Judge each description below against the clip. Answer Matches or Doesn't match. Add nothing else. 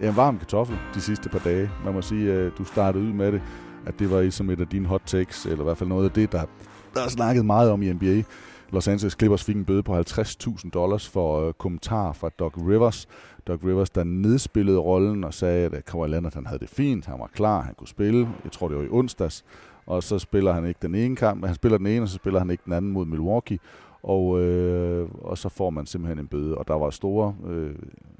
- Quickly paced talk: Matches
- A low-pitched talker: Matches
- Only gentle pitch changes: Doesn't match